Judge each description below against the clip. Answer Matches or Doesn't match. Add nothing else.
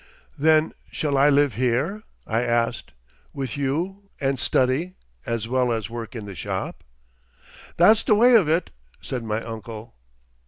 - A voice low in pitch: Matches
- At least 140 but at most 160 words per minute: Matches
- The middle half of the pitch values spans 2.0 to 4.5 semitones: Doesn't match